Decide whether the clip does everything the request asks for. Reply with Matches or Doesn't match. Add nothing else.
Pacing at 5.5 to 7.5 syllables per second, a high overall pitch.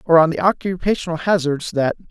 Doesn't match